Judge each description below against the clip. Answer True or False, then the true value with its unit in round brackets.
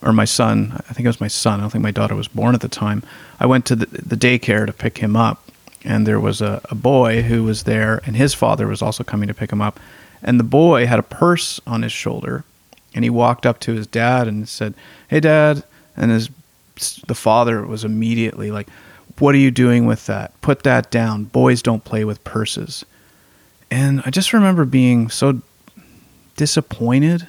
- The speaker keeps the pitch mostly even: False (3.4 semitones)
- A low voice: True (115 Hz)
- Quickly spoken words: True (210 wpm)